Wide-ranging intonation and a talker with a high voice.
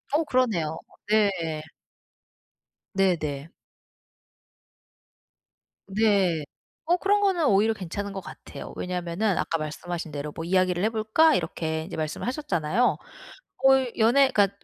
Yes: wide, 5.9 semitones; high, 195 Hz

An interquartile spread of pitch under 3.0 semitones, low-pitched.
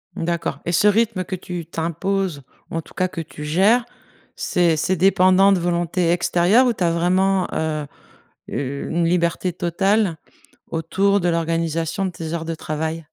No: narrow, 2.5 semitones; medium, 175 Hz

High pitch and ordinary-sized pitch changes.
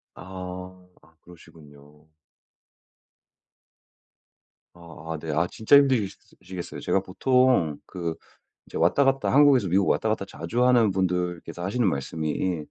No: very low, 90 Hz; average, 5.0 semitones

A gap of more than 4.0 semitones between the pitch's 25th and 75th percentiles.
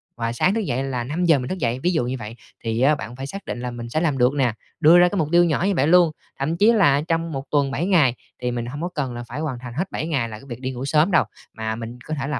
Yes: average, 5.2 semitones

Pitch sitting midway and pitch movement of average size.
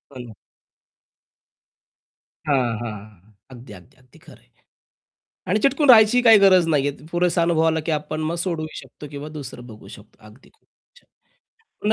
No: medium, 150 Hz; wide, 6.7 semitones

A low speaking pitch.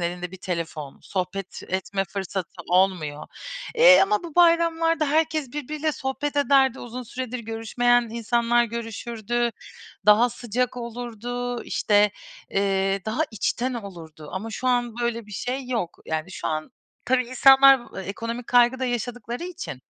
No: high, 235 Hz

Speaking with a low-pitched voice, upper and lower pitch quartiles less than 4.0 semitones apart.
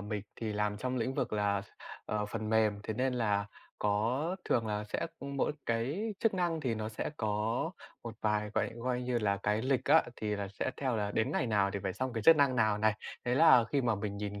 Yes: low, 110 Hz; average, 3.5 semitones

